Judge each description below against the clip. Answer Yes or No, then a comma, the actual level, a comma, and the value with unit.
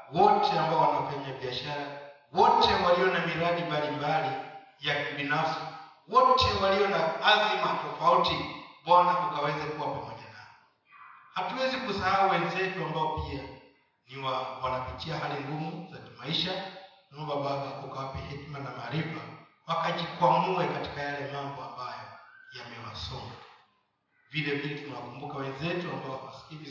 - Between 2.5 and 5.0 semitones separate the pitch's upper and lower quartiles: Yes, average, 4.3 semitones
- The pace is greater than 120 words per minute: No, average, 115 wpm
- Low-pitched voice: No, medium, 155 Hz